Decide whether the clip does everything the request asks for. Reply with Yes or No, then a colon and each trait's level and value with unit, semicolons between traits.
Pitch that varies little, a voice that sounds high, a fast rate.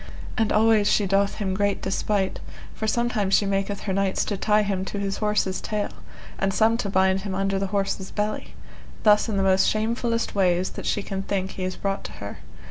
Yes: narrow, 1.7 semitones; high, 200 Hz; fast, 210 wpm